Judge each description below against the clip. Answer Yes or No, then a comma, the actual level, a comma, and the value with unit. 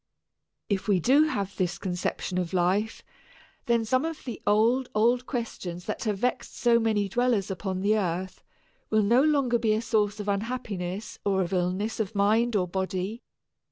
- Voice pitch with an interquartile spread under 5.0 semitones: Yes, average, 3.8 semitones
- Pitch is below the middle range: No, high, 210 Hz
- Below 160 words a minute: No, average, 170 wpm